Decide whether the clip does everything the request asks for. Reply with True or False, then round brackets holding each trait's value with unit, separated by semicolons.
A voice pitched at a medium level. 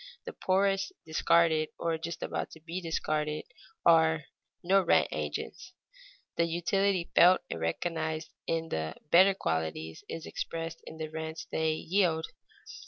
True (165 Hz)